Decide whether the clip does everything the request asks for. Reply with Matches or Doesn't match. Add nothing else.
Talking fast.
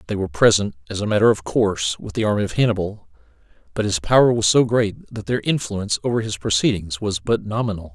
Matches